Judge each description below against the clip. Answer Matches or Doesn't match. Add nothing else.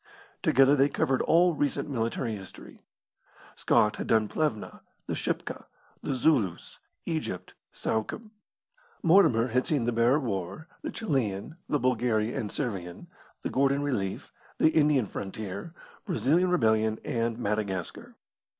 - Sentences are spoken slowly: Matches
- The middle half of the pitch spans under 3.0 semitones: Doesn't match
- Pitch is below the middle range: Matches